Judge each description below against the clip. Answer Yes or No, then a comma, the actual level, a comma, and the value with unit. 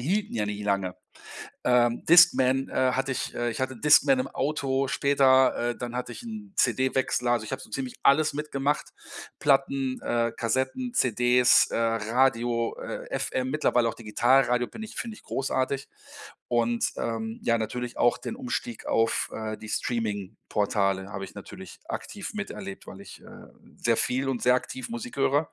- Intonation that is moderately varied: Yes, average, 3.0 semitones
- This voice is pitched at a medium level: No, low, 125 Hz